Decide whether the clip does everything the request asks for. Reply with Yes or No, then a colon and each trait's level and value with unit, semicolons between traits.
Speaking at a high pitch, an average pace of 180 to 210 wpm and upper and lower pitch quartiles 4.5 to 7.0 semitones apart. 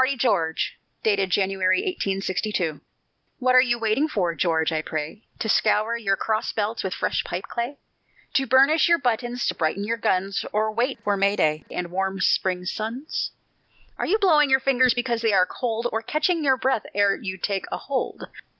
Yes: high, 220 Hz; average, 185 wpm; average, 5.1 semitones